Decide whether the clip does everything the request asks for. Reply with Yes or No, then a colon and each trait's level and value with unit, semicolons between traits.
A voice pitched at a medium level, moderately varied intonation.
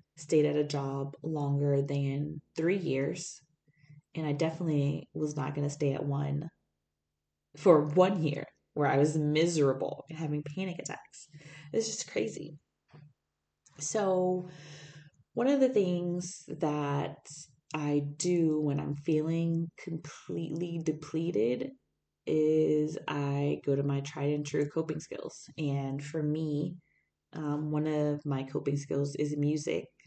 No: medium, 150 Hz; narrow, 1.9 semitones